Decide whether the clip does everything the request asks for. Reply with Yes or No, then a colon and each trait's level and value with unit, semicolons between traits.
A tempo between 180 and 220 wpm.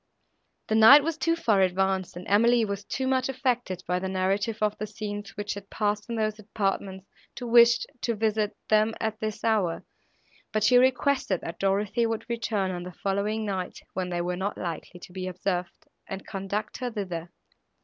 Yes: average, 185 wpm